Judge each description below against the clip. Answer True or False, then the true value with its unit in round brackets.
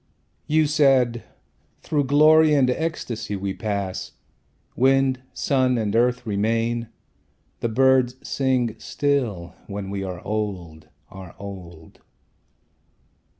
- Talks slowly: True (105 wpm)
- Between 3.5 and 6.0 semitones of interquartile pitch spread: True (5.1 semitones)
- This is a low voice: True (120 Hz)